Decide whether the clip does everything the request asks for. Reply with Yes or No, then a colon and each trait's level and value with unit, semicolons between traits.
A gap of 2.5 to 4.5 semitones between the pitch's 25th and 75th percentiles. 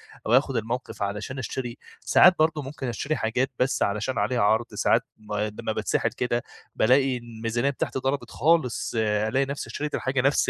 Yes: average, 3.5 semitones